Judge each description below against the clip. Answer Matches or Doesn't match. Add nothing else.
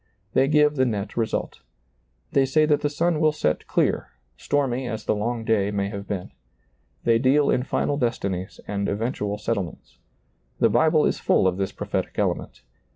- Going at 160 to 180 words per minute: Matches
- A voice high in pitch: Doesn't match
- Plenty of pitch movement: Matches